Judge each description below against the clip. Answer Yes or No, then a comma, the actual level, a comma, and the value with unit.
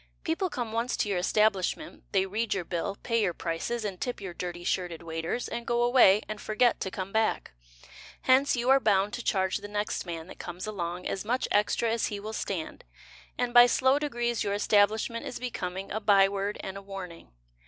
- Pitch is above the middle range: Yes, high, 205 Hz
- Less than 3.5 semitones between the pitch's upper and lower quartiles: No, average, 4.0 semitones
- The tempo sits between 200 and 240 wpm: Yes, fast, 205 wpm